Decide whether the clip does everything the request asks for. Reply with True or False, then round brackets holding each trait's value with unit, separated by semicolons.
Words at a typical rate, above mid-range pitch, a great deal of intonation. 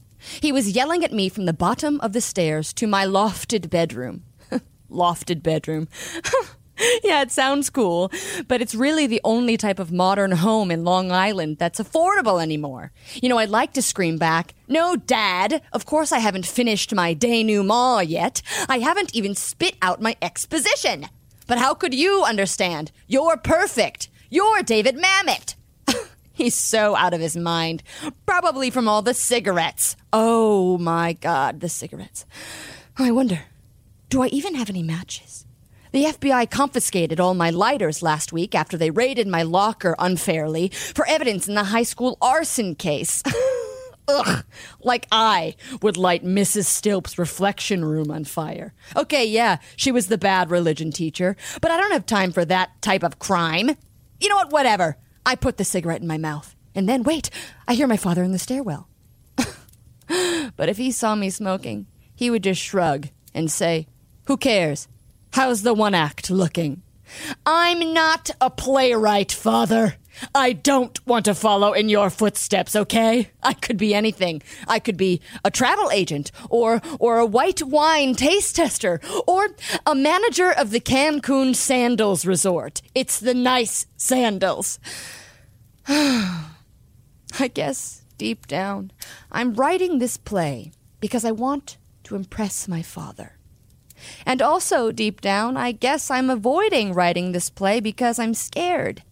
True (155 wpm; 215 Hz; 6.8 semitones)